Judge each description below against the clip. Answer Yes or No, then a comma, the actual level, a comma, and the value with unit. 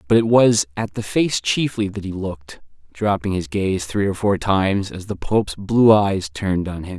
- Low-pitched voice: Yes, low, 100 Hz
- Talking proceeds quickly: Yes, fast, 215 wpm